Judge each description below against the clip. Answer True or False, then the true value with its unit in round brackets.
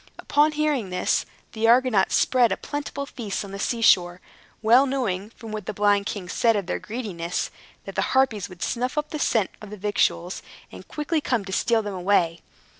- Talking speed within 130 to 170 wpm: False (195 wpm)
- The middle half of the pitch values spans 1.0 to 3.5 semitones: False (4.7 semitones)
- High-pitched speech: True (215 Hz)